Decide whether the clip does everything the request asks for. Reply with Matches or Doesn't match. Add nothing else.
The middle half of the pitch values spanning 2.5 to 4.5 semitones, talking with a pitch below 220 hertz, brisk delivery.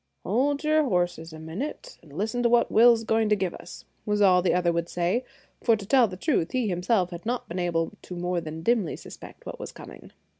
Doesn't match